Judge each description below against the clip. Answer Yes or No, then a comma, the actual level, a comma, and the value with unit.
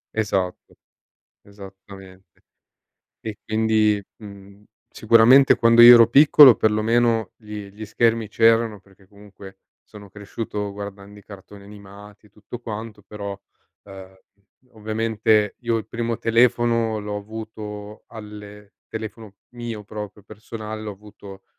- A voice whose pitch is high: No, low, 105 Hz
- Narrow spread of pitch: Yes, narrow, 1.8 semitones